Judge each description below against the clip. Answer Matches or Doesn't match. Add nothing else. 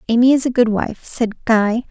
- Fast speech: Matches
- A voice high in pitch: Matches